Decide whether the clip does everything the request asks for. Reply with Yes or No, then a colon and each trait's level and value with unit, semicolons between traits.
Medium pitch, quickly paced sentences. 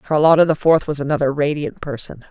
No: medium, 145 Hz; average, 180 wpm